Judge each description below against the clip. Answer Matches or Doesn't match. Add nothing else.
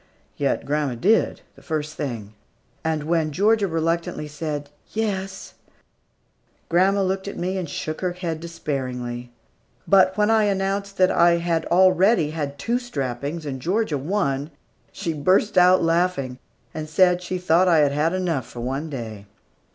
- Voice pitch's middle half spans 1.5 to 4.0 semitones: Doesn't match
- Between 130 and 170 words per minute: Matches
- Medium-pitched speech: Matches